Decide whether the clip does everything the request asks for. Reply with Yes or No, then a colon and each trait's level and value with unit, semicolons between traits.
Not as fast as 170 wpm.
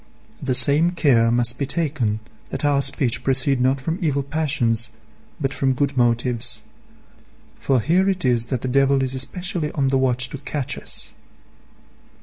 Yes: average, 160 wpm